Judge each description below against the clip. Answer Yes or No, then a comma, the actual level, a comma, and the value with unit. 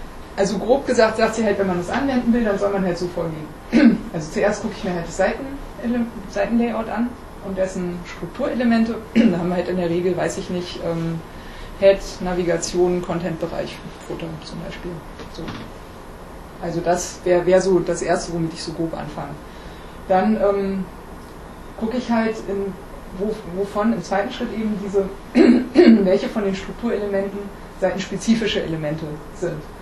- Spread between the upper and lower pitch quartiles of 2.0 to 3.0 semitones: No, average, 3.6 semitones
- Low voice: No, high, 195 Hz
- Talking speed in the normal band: Yes, average, 160 wpm